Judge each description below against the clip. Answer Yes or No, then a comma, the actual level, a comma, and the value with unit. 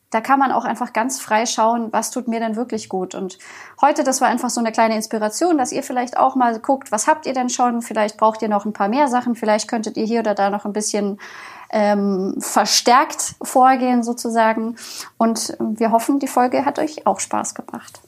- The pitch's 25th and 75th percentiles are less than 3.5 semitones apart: Yes, narrow, 2.6 semitones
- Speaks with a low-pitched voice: No, high, 230 Hz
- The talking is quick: Yes, fast, 215 wpm